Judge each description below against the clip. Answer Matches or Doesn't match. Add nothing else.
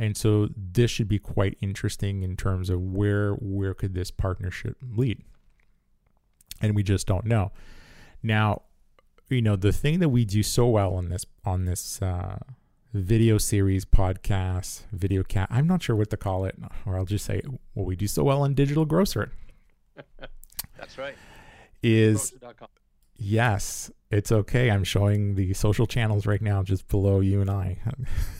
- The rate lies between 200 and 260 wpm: Doesn't match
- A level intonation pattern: Doesn't match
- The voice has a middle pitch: Doesn't match